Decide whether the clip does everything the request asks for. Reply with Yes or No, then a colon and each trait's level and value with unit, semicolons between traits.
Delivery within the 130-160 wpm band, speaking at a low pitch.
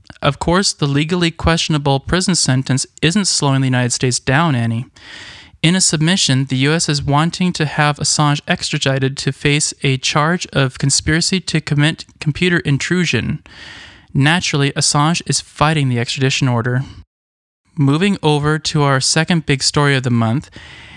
No: average, 150 wpm; medium, 145 Hz